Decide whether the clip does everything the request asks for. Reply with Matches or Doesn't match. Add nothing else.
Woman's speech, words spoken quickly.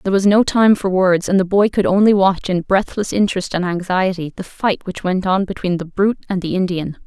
Matches